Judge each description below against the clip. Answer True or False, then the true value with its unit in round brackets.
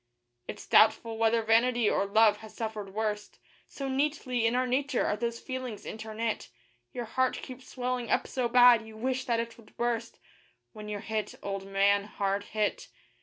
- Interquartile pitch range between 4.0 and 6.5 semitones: False (2.7 semitones)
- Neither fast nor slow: True (170 wpm)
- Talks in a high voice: True (225 Hz)